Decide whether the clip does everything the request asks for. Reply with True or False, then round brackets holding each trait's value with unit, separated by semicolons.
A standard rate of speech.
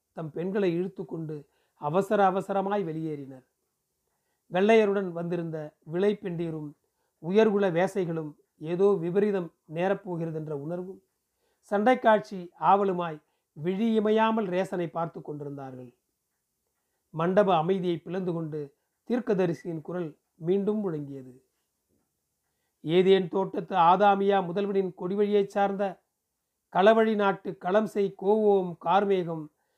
True (85 wpm)